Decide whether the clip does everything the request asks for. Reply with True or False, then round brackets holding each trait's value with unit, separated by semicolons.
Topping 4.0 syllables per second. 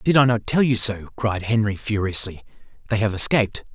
True (5.4 syllables/s)